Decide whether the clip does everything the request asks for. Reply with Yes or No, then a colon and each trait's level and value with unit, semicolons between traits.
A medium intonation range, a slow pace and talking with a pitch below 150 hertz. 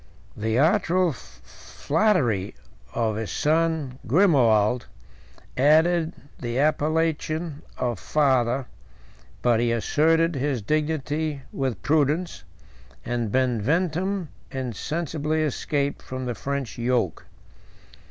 Yes: average, 4.7 semitones; slow, 90 wpm; medium, 140 Hz